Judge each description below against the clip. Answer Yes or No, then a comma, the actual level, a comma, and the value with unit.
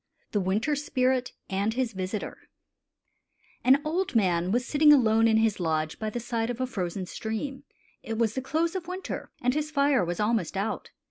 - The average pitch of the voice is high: Yes, high, 230 Hz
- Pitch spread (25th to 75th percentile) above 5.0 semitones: Yes, wide, 5.5 semitones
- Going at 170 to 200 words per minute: Yes, average, 185 wpm